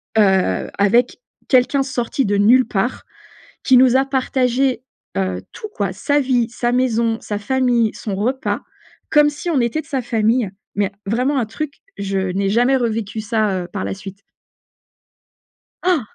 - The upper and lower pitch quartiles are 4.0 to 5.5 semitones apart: Yes, average, 4.4 semitones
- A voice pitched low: No, high, 235 Hz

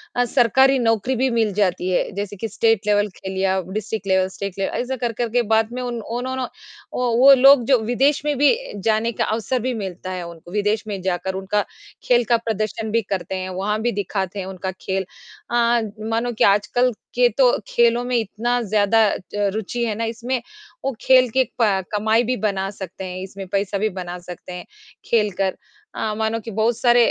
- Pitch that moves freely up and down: No, average, 3.8 semitones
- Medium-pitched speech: No, high, 220 Hz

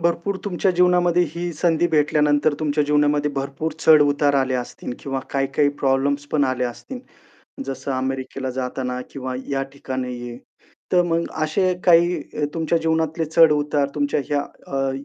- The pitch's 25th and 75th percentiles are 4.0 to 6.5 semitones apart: No, average, 3.3 semitones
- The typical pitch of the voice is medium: Yes, medium, 145 Hz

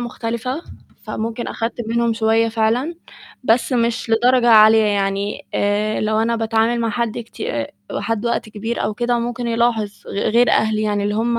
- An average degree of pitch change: No, narrow, 1.6 semitones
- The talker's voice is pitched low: No, high, 225 Hz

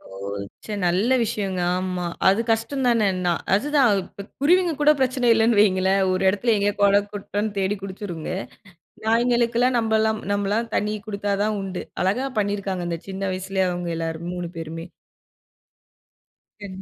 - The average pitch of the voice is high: Yes, high, 205 Hz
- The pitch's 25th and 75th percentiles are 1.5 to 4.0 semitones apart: Yes, average, 3.4 semitones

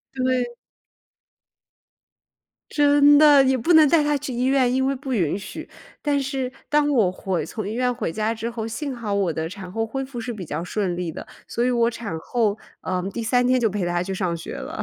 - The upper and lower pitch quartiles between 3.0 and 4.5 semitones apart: No, average, 5.2 semitones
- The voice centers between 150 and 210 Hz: No, high, 235 Hz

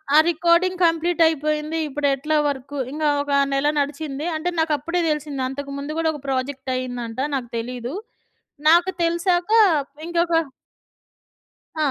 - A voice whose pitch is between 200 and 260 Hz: No, very high, 300 Hz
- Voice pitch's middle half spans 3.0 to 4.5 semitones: Yes, average, 3.5 semitones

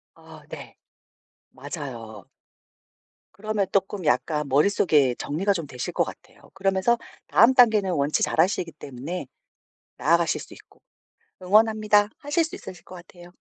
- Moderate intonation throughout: No, wide, 5.8 semitones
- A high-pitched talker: No, medium, 180 Hz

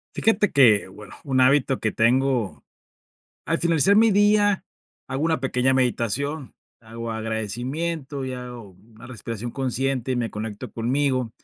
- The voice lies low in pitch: Yes, low, 130 Hz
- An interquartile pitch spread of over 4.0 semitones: No, average, 3.7 semitones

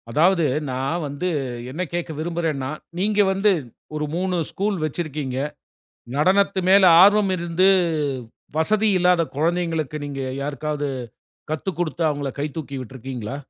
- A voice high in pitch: No, medium, 165 Hz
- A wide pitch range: No, average, 4.4 semitones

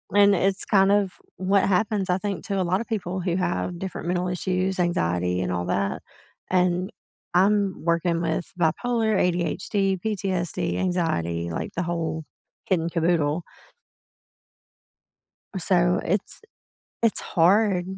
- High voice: No, medium, 180 Hz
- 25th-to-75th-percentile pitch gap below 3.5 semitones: Yes, narrow, 2.6 semitones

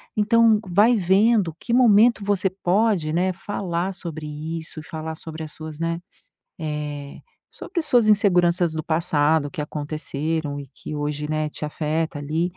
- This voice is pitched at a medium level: Yes, medium, 165 Hz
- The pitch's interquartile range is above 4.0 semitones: Yes, average, 4.7 semitones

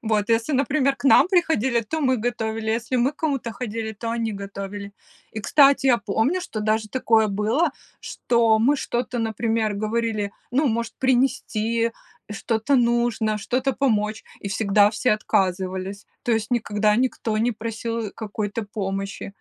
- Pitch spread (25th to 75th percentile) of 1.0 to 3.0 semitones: Yes, narrow, 2.6 semitones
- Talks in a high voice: Yes, high, 225 Hz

